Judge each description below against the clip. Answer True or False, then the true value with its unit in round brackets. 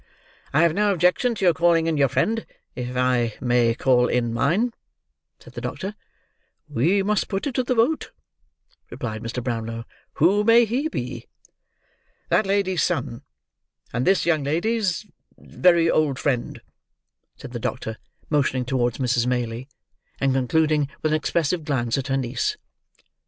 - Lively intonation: True (7.6 semitones)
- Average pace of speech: True (150 wpm)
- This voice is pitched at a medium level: True (150 Hz)